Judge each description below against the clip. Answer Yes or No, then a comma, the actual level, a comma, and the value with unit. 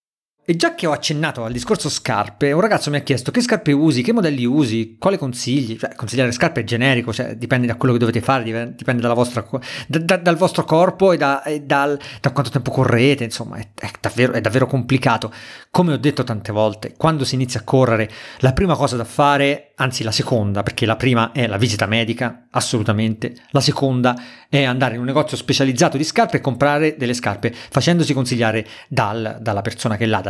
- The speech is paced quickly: Yes, fast, 205 wpm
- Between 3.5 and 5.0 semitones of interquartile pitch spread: Yes, average, 3.8 semitones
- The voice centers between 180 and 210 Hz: No, low, 130 Hz